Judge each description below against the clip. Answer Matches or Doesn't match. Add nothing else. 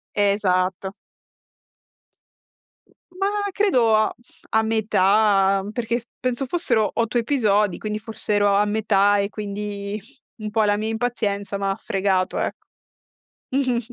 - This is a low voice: Doesn't match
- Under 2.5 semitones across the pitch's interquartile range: Matches